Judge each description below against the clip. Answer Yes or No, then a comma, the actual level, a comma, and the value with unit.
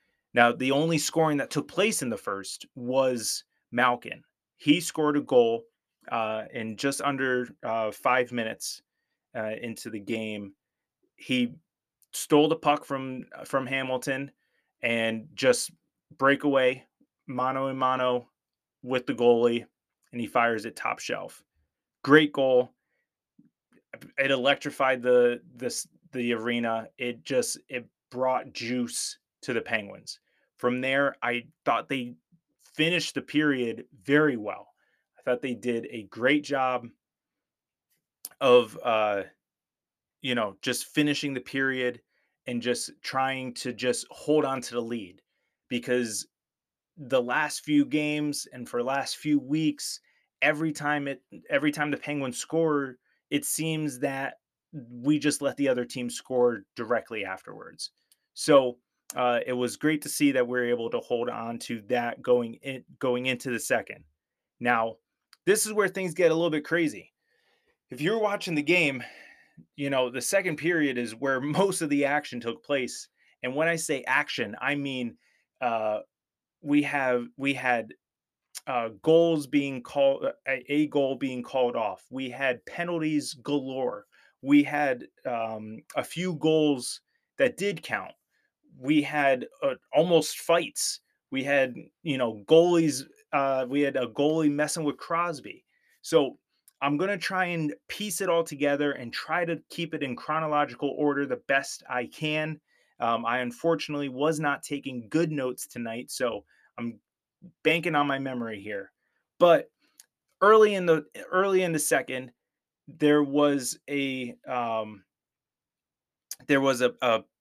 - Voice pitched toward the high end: No, medium, 140 Hz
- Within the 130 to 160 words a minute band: Yes, average, 145 wpm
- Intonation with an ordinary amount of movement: Yes, average, 3.9 semitones